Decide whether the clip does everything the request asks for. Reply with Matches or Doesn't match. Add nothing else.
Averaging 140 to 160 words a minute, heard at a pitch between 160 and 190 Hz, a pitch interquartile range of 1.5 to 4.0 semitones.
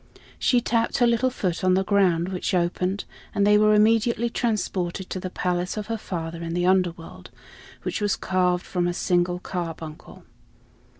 Doesn't match